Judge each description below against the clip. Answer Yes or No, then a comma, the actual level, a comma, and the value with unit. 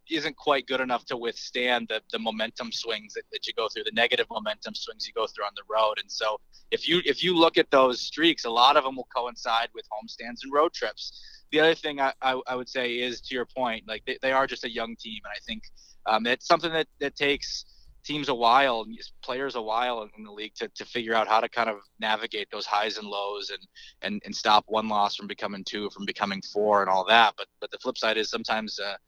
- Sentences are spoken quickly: Yes, fast, 250 wpm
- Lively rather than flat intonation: Yes, wide, 6.0 semitones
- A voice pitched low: Yes, low, 125 Hz